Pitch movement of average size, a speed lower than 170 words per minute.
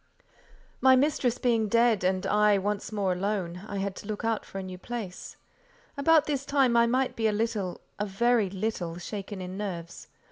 No: average, 3.7 semitones; average, 175 wpm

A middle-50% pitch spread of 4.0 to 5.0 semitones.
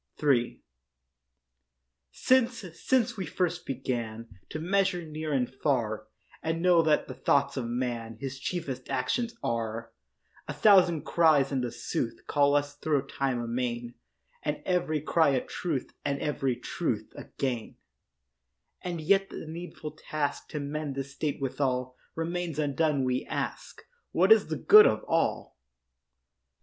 Yes: average, 4.5 semitones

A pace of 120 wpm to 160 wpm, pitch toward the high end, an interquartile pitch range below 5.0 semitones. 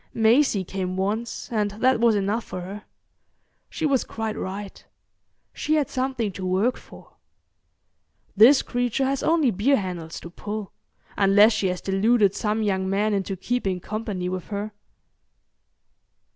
Yes: average, 145 wpm; high, 210 Hz; average, 3.6 semitones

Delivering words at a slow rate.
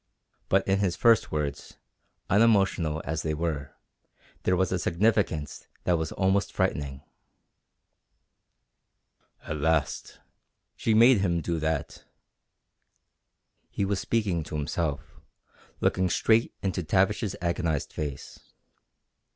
Yes: slow, 110 wpm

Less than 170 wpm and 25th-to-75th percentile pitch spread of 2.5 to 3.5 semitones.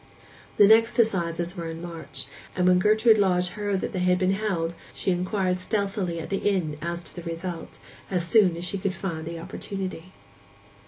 No: average, 180 wpm; average, 2.8 semitones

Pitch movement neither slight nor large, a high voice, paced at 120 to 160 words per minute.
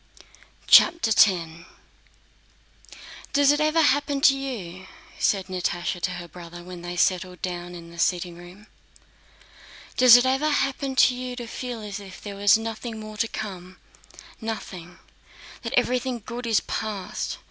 No: wide, 5.9 semitones; high, 215 Hz; average, 145 wpm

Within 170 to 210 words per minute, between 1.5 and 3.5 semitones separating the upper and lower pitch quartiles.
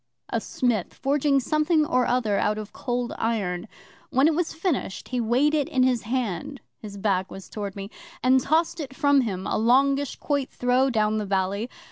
No: average, 185 wpm; average, 4.8 semitones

